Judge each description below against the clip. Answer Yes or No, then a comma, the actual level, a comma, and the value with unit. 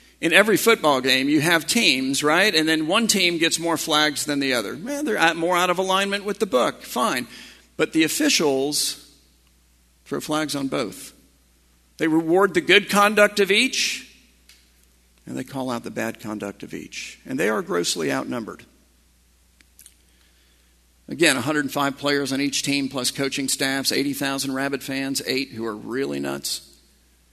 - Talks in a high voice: No, medium, 140 Hz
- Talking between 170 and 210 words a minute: No, average, 160 wpm